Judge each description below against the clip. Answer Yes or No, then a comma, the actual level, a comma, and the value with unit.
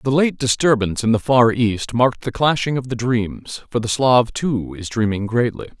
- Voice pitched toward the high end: No, low, 120 Hz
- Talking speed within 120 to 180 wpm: No, fast, 205 wpm